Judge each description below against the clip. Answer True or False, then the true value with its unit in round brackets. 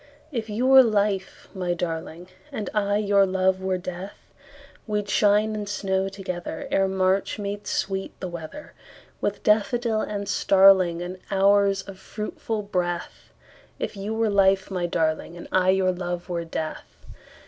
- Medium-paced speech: False (125 wpm)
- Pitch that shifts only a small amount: True (2.2 semitones)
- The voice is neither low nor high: False (195 Hz)